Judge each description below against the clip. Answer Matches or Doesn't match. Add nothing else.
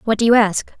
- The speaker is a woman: Matches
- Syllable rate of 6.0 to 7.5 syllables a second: Matches